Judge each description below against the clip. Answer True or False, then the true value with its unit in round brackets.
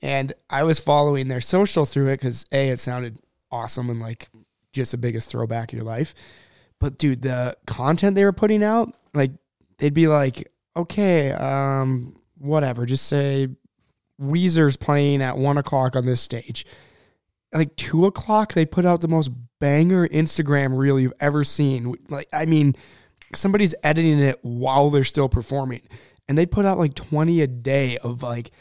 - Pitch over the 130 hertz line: True (140 Hz)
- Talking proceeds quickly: False (170 wpm)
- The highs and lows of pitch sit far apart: False (3.8 semitones)